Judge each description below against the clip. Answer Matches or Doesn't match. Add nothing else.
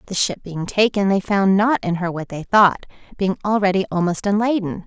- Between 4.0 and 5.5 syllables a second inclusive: Matches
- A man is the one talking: Doesn't match